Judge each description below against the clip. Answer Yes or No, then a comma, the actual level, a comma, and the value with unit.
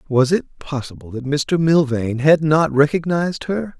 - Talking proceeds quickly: No, average, 160 wpm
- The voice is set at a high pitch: No, medium, 150 Hz